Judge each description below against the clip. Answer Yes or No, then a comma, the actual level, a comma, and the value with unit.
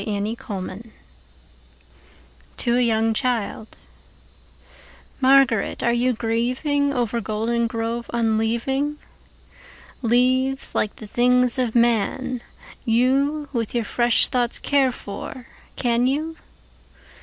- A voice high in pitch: Yes, high, 240 Hz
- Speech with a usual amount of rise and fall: No, narrow, 2.3 semitones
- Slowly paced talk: Yes, slow, 85 wpm